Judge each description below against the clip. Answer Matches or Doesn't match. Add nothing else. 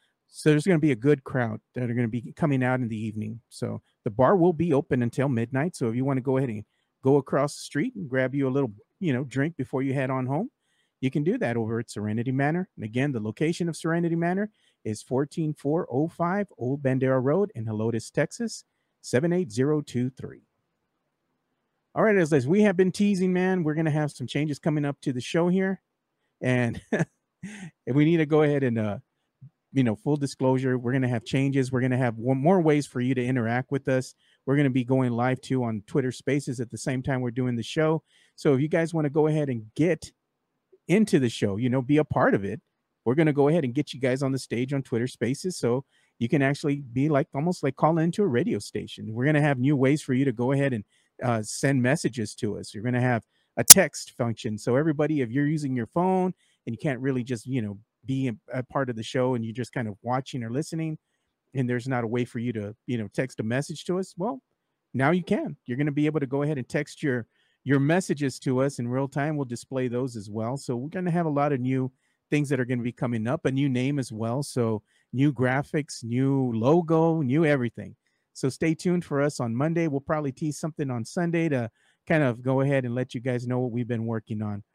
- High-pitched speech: Doesn't match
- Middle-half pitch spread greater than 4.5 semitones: Doesn't match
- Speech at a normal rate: Doesn't match